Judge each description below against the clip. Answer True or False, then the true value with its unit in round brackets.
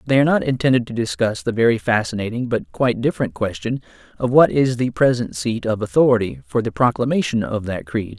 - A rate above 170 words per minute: True (200 wpm)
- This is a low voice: True (120 Hz)